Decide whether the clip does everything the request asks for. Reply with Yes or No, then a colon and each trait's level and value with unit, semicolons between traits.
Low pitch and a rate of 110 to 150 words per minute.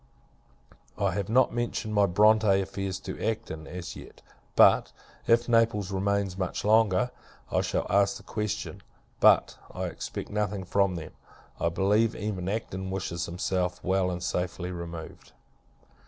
Yes: low, 100 Hz; average, 140 wpm